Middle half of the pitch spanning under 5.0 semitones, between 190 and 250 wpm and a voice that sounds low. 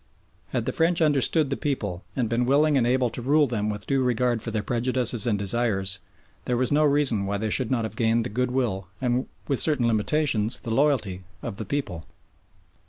Yes: average, 3.9 semitones; average, 200 wpm; low, 120 Hz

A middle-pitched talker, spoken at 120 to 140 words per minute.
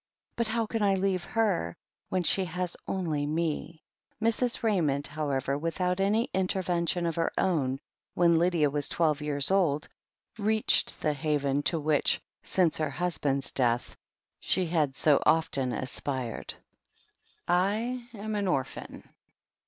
Yes: medium, 165 Hz; slow, 135 wpm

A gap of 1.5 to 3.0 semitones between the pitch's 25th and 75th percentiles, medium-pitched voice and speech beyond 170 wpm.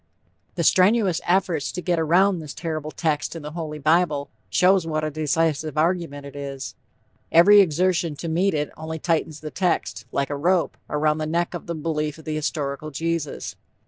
Yes: narrow, 2.5 semitones; medium, 160 Hz; average, 180 wpm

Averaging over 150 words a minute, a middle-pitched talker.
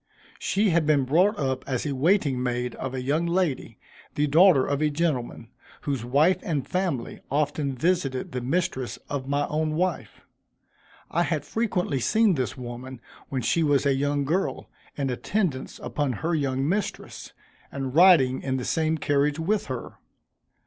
Yes: average, 165 wpm; medium, 145 Hz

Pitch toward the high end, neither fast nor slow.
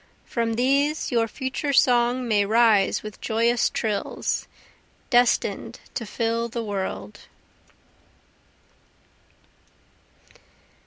No: high, 230 Hz; slow, 85 wpm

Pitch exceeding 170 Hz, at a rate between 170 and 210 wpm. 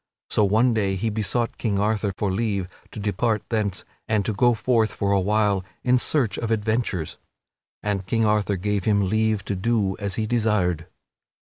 No: low, 105 Hz; average, 180 wpm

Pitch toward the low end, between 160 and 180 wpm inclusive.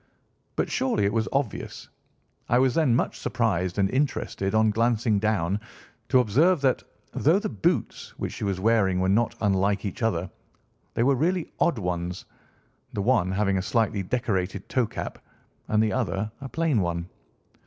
Yes: low, 110 Hz; average, 165 wpm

